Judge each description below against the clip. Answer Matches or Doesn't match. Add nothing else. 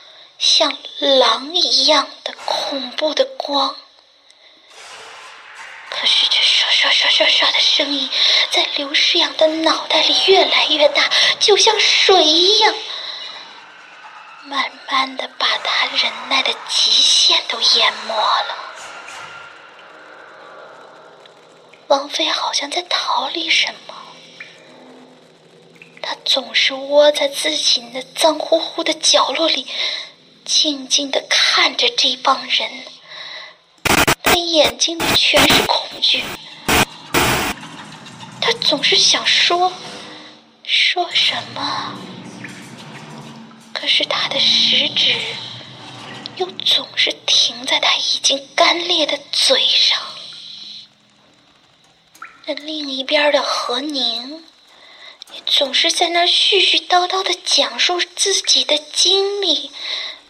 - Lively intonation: Doesn't match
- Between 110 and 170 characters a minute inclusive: Matches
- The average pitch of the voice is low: Doesn't match